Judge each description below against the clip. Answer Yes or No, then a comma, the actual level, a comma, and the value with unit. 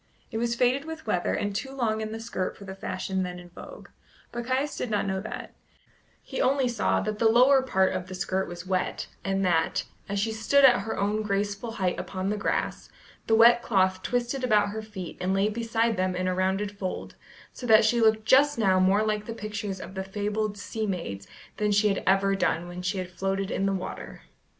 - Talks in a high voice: Yes, high, 205 Hz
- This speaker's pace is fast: Yes, fast, 220 wpm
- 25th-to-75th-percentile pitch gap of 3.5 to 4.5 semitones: No, average, 3.1 semitones